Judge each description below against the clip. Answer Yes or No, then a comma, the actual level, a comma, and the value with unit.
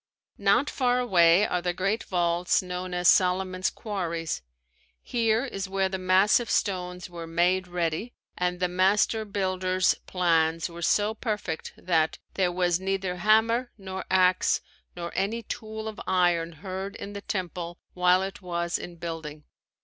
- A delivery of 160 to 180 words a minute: No, average, 150 wpm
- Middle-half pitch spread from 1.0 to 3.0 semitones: Yes, narrow, 2.4 semitones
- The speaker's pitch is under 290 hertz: Yes, medium, 185 Hz